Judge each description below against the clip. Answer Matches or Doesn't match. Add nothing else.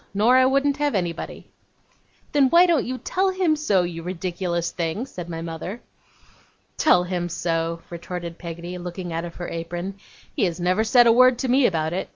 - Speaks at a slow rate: Doesn't match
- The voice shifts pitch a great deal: Matches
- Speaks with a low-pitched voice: Doesn't match